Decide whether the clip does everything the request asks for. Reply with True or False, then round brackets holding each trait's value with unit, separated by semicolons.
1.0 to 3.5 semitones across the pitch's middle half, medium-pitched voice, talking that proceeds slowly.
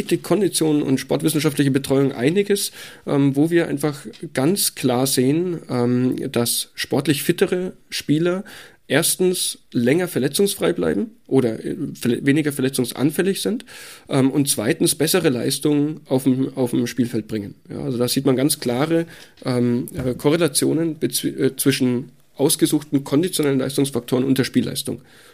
False (4.1 semitones; 145 Hz; 110 wpm)